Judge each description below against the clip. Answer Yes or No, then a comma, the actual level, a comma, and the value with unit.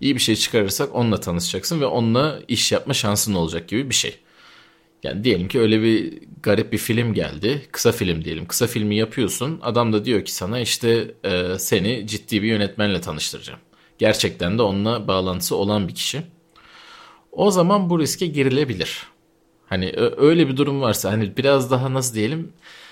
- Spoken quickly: Yes, fast, 165 wpm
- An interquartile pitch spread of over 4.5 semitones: Yes, average, 5.2 semitones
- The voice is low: Yes, low, 115 Hz